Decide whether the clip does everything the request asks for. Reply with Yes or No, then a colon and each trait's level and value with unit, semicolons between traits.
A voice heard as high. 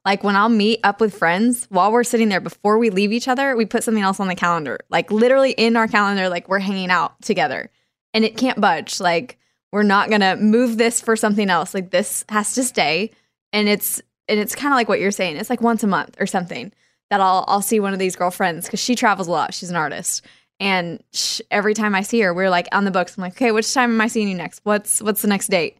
Yes: high, 210 Hz